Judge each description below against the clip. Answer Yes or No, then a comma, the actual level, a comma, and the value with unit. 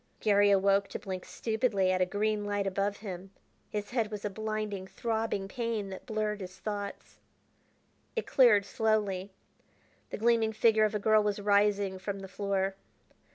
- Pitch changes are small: Yes, narrow, 1.7 semitones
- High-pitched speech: Yes, high, 205 Hz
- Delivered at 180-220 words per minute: No, average, 160 wpm